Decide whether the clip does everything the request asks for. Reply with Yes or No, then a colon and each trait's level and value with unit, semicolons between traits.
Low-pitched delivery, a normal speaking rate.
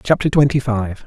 Yes: low, 125 Hz; average, 170 wpm